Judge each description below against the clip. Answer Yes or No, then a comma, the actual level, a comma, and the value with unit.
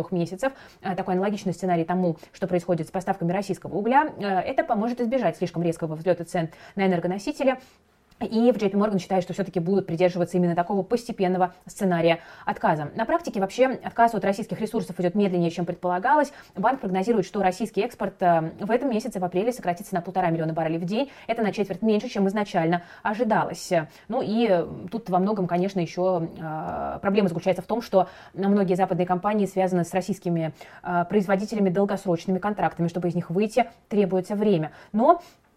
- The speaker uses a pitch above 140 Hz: Yes, high, 190 Hz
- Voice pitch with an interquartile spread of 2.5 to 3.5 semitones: Yes, average, 3.1 semitones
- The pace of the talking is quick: Yes, fast, 165 wpm